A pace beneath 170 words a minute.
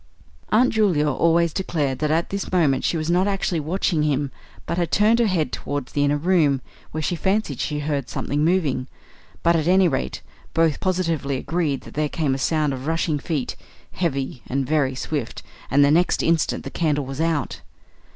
No: average, 190 wpm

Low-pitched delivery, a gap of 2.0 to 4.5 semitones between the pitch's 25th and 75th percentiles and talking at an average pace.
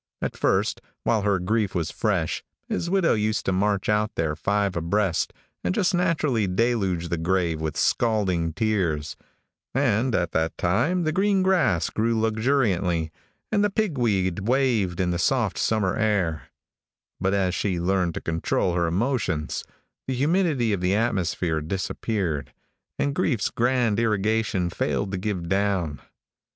No: low, 100 Hz; average, 5.1 semitones; average, 150 wpm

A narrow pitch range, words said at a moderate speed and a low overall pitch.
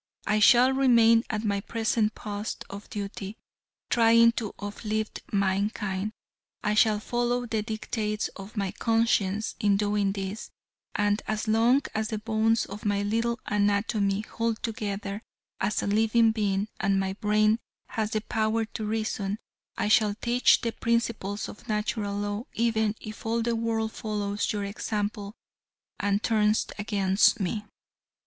No: narrow, 1.7 semitones; average, 145 wpm; high, 215 Hz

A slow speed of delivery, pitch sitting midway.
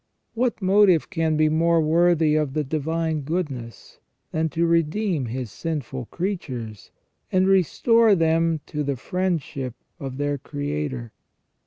Yes: slow, 130 wpm; medium, 160 Hz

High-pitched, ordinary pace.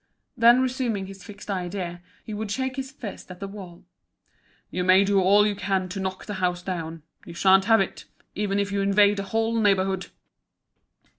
Yes: high, 195 Hz; average, 190 wpm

